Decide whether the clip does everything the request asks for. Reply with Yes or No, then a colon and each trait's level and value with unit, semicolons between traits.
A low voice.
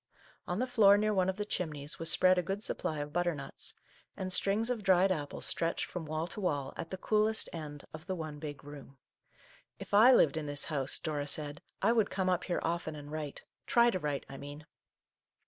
No: medium, 165 Hz